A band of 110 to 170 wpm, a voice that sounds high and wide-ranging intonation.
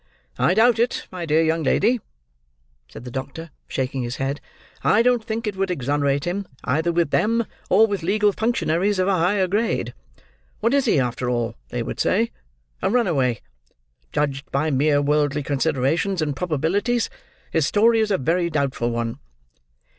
No: average, 165 wpm; medium, 165 Hz; wide, 7.0 semitones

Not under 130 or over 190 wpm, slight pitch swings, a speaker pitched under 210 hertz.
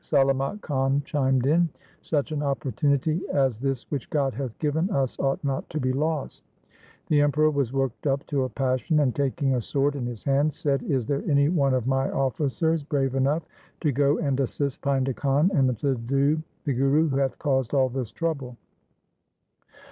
Yes: average, 185 wpm; narrow, 1.8 semitones; medium, 140 Hz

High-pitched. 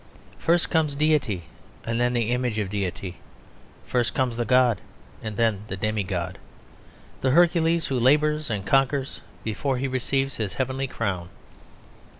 No: low, 125 Hz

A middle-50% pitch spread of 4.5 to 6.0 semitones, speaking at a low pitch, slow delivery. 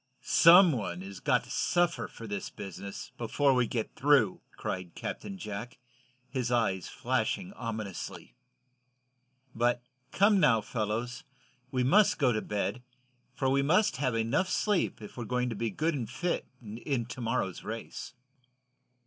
No: average, 4.9 semitones; low, 120 Hz; average, 145 wpm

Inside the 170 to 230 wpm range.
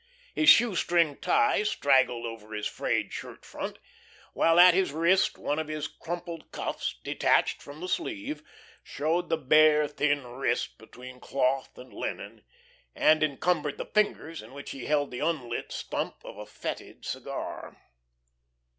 No: average, 145 wpm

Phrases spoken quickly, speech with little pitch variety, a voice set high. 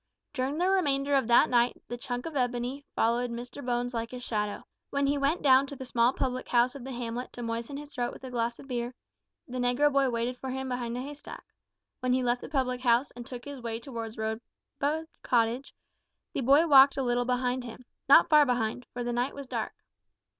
Yes: fast, 220 wpm; narrow, 2.2 semitones; very high, 250 Hz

